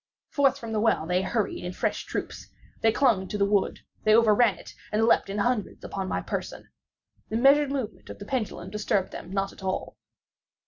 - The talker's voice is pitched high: Yes, high, 210 Hz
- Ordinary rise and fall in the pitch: Yes, average, 3.3 semitones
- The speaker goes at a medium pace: Yes, average, 190 wpm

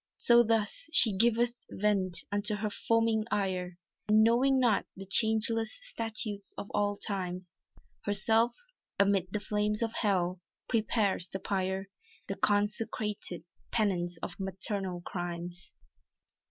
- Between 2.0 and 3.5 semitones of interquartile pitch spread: Yes, average, 2.8 semitones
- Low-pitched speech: No, high, 205 Hz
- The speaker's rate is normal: No, slow, 120 wpm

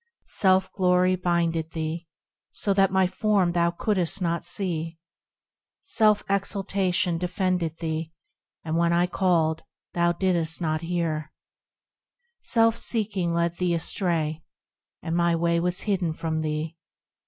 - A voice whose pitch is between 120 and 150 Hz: No, medium, 175 Hz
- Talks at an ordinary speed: No, slow, 125 wpm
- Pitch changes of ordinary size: No, narrow, 2.2 semitones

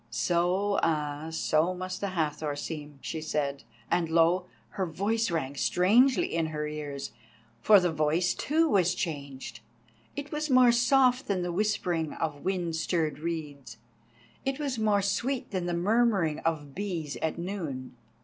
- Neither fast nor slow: Yes, average, 150 wpm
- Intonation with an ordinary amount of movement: Yes, average, 5.0 semitones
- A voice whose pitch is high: No, medium, 170 Hz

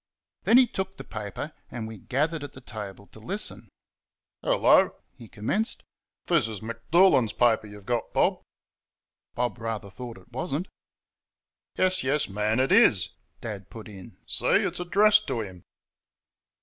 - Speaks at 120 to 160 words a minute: Yes, average, 150 wpm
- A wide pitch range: Yes, wide, 6.6 semitones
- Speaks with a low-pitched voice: Yes, low, 115 Hz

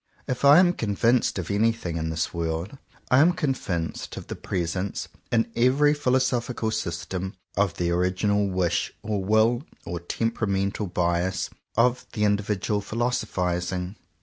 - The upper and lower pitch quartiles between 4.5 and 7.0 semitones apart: Yes, average, 4.9 semitones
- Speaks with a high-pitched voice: No, low, 100 Hz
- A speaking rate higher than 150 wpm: No, average, 140 wpm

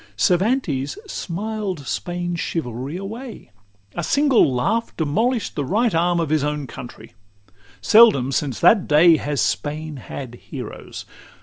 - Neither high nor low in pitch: Yes, medium, 165 Hz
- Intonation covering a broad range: Yes, wide, 7.0 semitones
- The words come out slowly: Yes, slow, 130 wpm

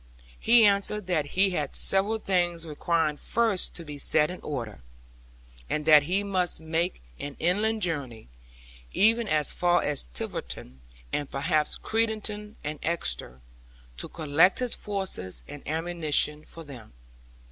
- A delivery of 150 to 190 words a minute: No, slow, 135 wpm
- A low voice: No, medium, 165 Hz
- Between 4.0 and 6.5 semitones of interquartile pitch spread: Yes, average, 5.1 semitones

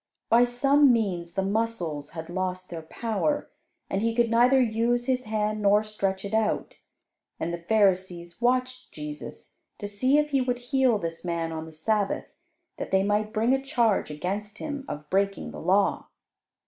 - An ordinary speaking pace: Yes, average, 175 wpm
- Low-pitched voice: No, high, 210 Hz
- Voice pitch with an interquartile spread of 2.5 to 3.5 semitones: No, average, 4.9 semitones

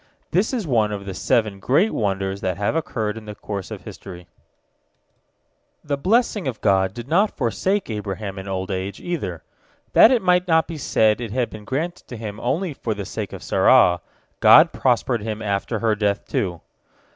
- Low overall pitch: Yes, low, 110 Hz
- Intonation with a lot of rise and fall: Yes, wide, 7.4 semitones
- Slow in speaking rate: No, average, 185 wpm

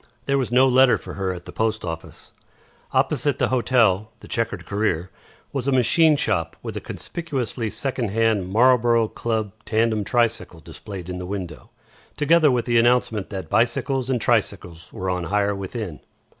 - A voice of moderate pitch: No, low, 110 Hz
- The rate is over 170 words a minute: No, average, 165 wpm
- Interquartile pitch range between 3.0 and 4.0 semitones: No, average, 4.5 semitones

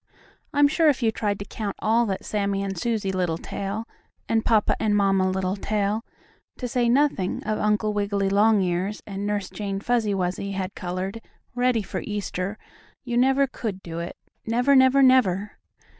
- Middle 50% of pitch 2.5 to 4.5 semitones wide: Yes, average, 3.2 semitones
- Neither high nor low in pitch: No, high, 205 Hz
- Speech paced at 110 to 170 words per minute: Yes, average, 160 wpm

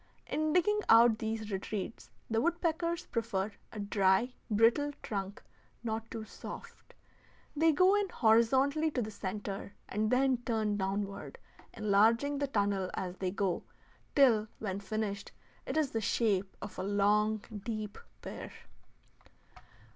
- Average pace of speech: No, slow, 130 wpm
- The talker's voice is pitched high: Yes, high, 220 Hz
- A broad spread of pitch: No, average, 4.7 semitones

